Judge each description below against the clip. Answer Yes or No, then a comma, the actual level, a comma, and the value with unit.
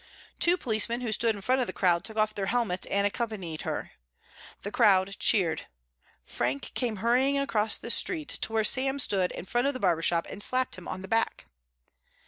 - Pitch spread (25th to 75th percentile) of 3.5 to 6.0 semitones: Yes, average, 4.4 semitones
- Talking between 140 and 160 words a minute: No, average, 200 wpm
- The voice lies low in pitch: No, high, 215 Hz